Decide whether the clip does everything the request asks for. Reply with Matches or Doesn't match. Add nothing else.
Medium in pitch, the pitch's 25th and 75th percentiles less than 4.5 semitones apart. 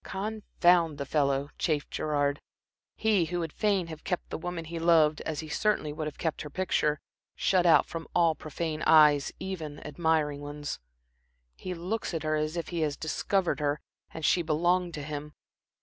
Matches